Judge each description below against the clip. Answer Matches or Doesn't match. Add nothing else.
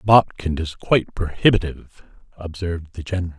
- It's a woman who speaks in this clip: Doesn't match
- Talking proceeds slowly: Matches